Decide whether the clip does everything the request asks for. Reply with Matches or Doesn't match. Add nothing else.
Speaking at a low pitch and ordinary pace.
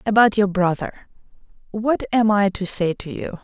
Doesn't match